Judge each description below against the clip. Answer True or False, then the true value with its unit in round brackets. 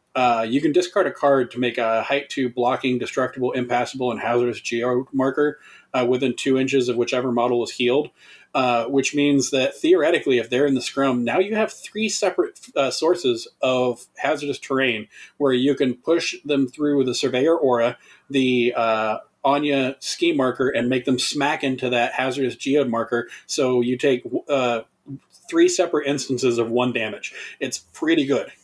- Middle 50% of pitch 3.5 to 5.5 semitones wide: False (2.7 semitones)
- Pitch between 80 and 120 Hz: False (130 Hz)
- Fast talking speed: False (175 wpm)